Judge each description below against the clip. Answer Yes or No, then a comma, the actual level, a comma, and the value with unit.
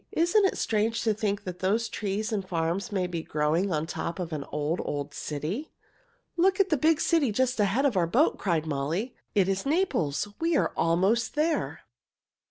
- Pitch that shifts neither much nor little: No, wide, 7.7 semitones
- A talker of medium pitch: No, high, 200 Hz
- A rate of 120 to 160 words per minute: No, average, 185 wpm